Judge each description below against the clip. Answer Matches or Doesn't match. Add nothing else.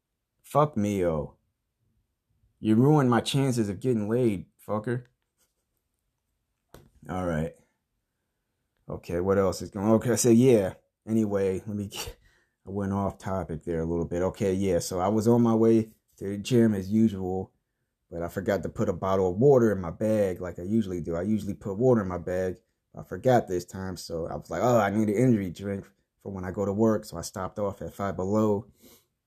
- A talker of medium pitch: Doesn't match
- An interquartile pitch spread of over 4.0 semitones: Doesn't match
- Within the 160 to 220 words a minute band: Matches